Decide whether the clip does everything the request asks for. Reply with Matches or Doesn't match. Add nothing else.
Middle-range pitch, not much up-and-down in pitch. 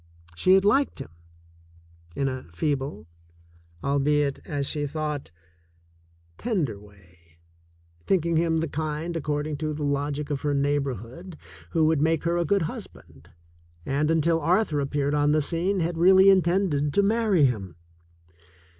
Doesn't match